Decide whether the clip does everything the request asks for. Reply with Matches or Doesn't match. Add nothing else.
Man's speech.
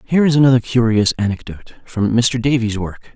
Matches